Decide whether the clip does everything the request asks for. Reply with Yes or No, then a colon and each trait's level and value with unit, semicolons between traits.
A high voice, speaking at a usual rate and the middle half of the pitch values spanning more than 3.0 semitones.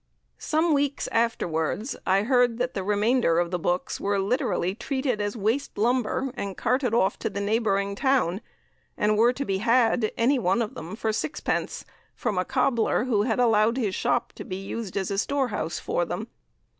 Yes: high, 225 Hz; average, 185 wpm; average, 4.2 semitones